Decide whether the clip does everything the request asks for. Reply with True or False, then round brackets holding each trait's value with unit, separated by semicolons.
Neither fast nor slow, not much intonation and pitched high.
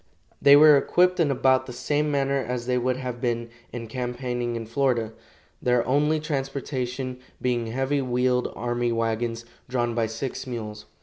False (160 wpm; 2.3 semitones; 125 Hz)